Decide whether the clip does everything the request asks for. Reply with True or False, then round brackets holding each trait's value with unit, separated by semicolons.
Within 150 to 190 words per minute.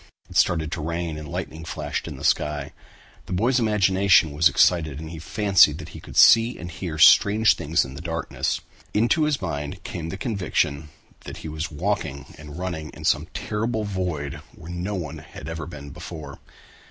True (185 wpm)